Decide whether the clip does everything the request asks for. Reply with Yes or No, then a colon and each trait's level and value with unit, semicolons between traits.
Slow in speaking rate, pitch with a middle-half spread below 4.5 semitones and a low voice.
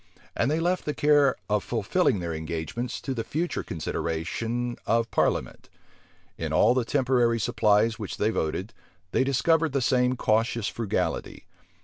No: average, 145 wpm; average, 4.1 semitones; low, 115 Hz